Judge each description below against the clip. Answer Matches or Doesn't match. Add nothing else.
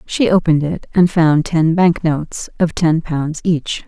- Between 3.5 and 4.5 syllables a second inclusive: Matches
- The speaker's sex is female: Matches